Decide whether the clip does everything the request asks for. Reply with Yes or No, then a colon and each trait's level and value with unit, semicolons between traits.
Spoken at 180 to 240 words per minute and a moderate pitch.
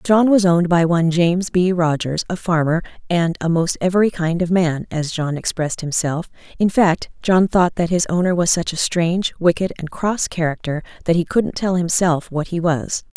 Yes: average, 200 wpm; medium, 175 Hz